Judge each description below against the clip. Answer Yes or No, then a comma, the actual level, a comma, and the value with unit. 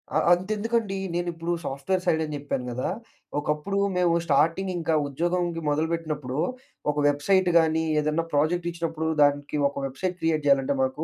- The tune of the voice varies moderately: Yes, average, 3.3 semitones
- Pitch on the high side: No, medium, 160 Hz